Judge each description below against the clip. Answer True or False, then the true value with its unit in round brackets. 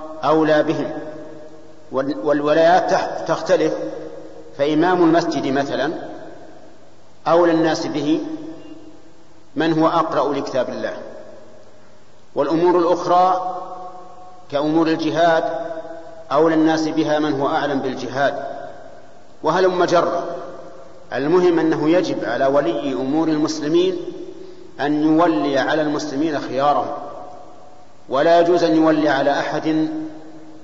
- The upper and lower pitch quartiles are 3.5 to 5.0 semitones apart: False (2.9 semitones)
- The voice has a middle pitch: True (165 Hz)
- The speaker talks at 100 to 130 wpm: False (90 wpm)